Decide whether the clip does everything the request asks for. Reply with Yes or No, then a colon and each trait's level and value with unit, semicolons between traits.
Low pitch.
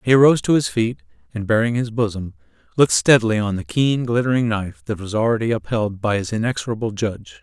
Yes: low, 110 Hz